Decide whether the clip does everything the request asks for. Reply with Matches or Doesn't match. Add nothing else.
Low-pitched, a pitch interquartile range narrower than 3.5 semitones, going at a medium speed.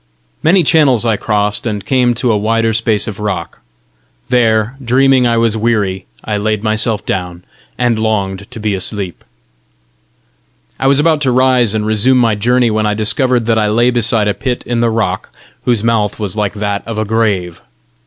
Matches